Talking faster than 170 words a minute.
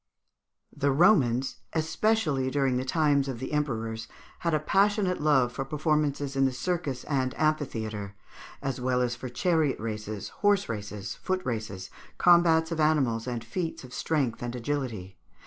No: average, 150 wpm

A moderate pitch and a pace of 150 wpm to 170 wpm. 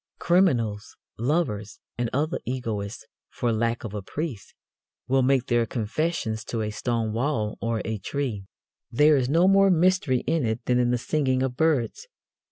No: low, 125 Hz; average, 165 wpm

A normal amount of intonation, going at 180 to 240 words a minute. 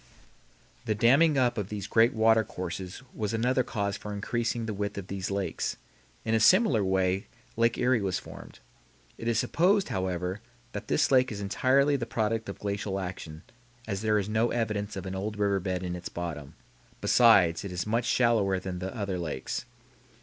Yes: average, 3.5 semitones; average, 185 wpm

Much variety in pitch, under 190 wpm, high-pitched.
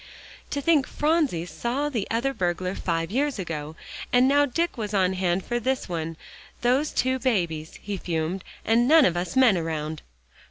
Yes: wide, 7.4 semitones; average, 170 wpm; high, 205 Hz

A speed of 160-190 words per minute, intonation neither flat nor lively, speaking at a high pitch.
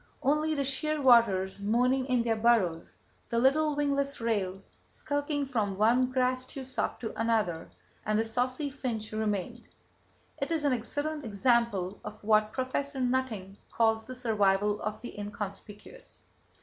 No: slow, 135 wpm; average, 4.1 semitones; high, 235 Hz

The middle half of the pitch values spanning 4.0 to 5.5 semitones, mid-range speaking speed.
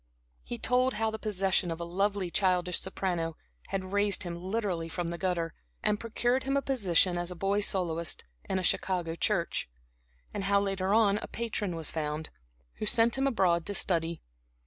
No: average, 3.4 semitones; average, 175 wpm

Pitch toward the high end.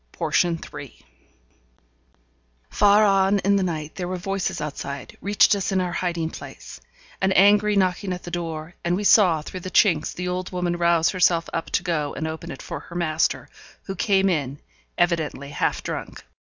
No: medium, 175 Hz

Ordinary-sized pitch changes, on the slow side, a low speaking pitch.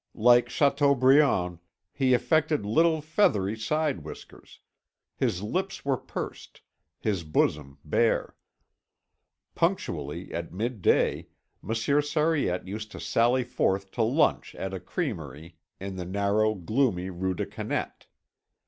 No: wide, 7.1 semitones; slow, 115 wpm; low, 110 Hz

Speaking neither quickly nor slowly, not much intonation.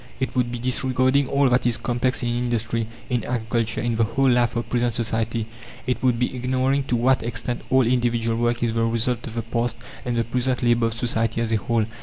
No: fast, 220 wpm; narrow, 1.5 semitones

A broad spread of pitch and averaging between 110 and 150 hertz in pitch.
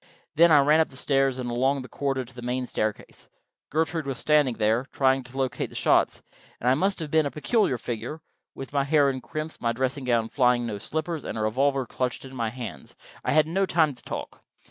No: average, 3.7 semitones; low, 135 Hz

